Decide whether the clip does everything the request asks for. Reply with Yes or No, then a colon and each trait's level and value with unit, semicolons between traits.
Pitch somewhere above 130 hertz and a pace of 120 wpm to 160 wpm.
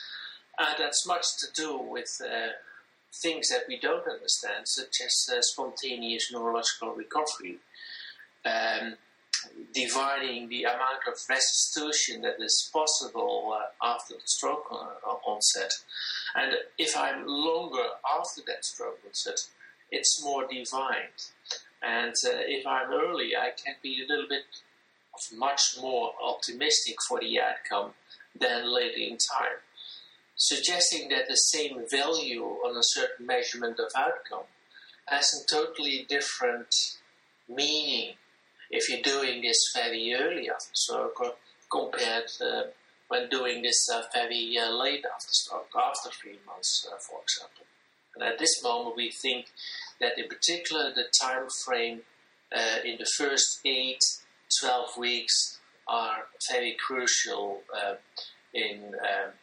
Yes: medium, 140 Hz; slow, 135 wpm